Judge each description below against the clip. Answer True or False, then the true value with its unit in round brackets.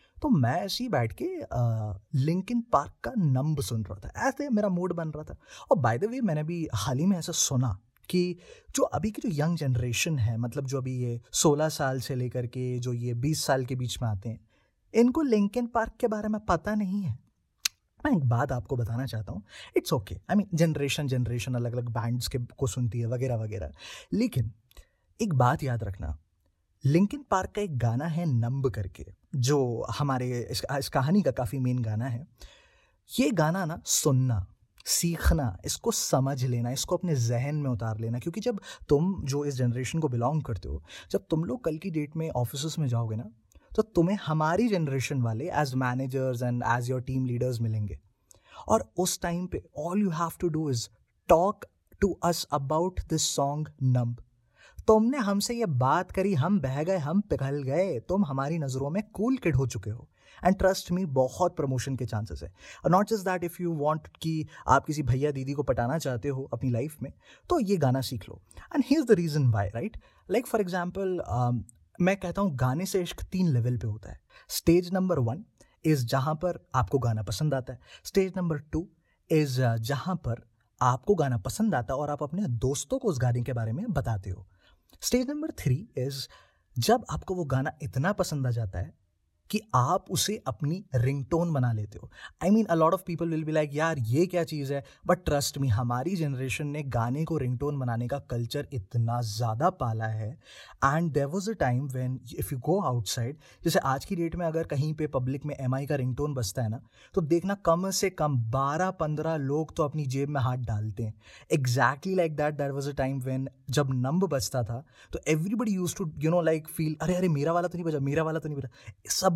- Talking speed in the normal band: False (205 wpm)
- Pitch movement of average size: False (6.0 semitones)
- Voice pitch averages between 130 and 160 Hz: True (140 Hz)